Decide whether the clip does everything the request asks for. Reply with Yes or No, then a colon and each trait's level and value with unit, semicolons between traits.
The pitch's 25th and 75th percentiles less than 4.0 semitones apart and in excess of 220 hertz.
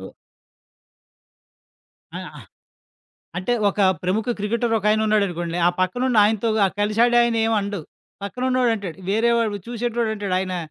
No: average, 2.8 semitones; high, 215 Hz